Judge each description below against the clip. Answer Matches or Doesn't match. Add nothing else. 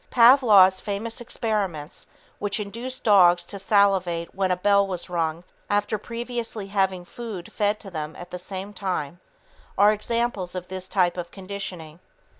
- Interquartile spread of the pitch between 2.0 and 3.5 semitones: Matches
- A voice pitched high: Matches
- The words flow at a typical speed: Matches